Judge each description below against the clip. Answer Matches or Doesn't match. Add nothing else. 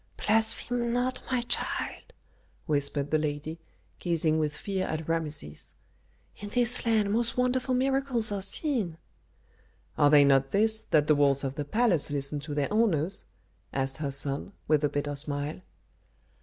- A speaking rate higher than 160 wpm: Doesn't match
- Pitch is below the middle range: Doesn't match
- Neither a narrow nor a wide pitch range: Doesn't match